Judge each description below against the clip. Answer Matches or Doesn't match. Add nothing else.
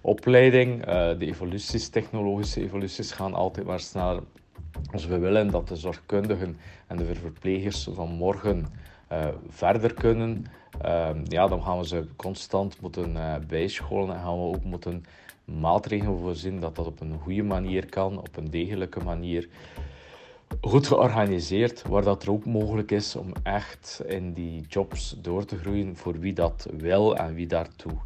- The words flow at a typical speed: Matches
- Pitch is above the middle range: Doesn't match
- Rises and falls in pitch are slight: Doesn't match